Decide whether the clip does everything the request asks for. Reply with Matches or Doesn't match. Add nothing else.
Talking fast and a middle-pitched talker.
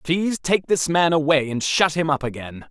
Matches